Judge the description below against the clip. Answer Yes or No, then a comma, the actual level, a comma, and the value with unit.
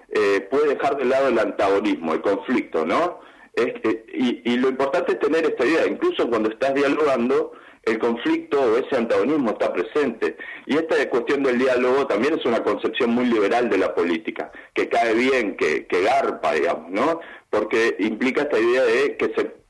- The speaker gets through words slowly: No, average, 185 wpm